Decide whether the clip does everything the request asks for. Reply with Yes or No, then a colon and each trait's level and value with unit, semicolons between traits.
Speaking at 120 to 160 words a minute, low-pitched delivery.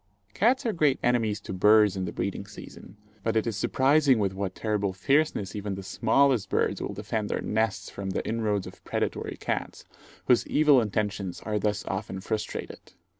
No: average, 175 wpm; low, 105 Hz